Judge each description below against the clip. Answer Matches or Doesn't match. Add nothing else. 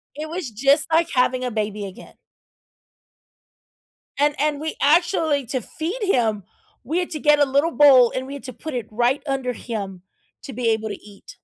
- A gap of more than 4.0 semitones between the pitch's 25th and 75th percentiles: Matches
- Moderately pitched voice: Doesn't match